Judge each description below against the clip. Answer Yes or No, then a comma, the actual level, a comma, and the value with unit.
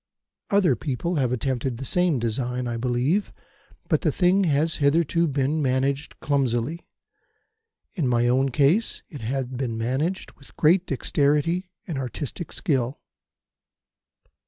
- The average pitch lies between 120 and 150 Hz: Yes, medium, 140 Hz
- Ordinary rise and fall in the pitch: Yes, average, 4.5 semitones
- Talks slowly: Yes, slow, 130 wpm